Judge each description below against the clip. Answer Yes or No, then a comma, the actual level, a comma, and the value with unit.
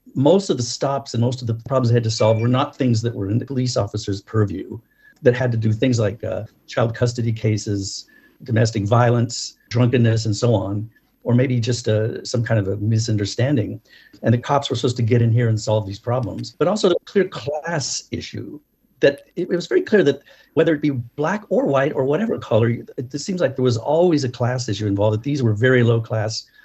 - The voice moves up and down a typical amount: Yes, average, 3.2 semitones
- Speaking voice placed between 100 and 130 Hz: Yes, low, 120 Hz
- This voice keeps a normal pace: No, fast, 220 wpm